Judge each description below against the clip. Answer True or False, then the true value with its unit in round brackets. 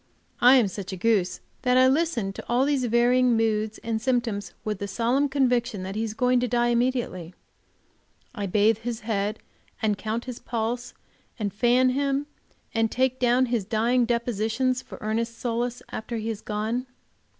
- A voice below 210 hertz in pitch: False (235 Hz)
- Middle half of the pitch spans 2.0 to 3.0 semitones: True (2.6 semitones)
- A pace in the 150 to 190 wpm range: True (175 wpm)